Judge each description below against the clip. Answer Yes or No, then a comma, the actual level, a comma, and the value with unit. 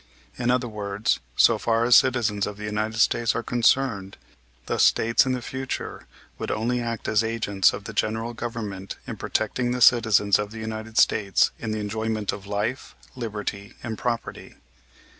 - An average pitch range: No, narrow, 2.3 semitones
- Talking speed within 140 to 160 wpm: No, average, 170 wpm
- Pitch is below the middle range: Yes, low, 110 Hz